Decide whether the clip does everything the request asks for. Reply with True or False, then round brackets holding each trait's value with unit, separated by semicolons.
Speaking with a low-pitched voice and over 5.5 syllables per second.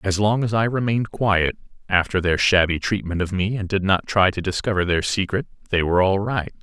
True (95 Hz; 5.7 syllables/s)